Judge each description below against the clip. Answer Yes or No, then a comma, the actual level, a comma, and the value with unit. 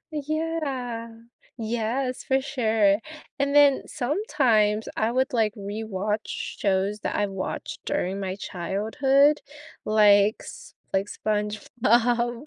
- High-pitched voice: Yes, high, 225 Hz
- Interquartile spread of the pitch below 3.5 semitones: No, average, 4.4 semitones